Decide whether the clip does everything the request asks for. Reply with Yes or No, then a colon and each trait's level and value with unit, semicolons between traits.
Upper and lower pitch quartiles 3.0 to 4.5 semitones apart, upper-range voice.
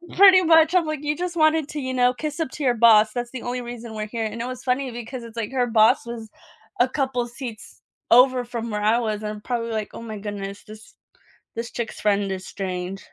Yes: average, 3.3 semitones; high, 240 Hz